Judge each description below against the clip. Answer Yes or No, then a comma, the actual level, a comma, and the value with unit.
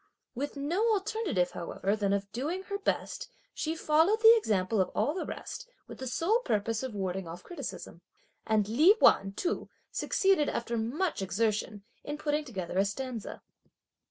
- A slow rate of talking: No, average, 165 wpm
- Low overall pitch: No, very high, 255 Hz